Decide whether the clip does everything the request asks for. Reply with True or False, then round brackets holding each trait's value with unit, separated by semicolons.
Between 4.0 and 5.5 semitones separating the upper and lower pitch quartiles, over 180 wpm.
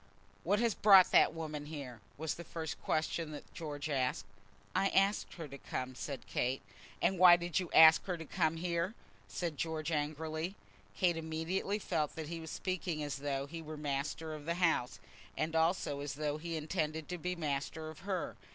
False (2.7 semitones; 190 wpm)